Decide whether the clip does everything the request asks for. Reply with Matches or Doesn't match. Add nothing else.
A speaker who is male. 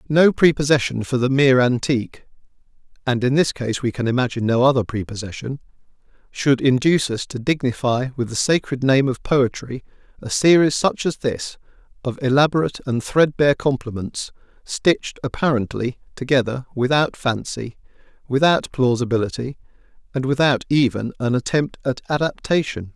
Matches